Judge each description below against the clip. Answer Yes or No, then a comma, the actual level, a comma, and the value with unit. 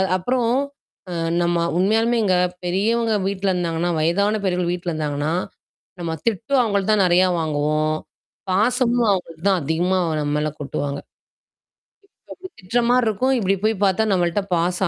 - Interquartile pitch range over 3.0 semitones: Yes, average, 4.4 semitones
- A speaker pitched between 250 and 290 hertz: No, medium, 185 Hz